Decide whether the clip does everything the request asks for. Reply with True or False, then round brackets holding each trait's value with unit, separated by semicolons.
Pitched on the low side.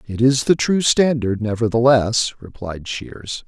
True (120 Hz)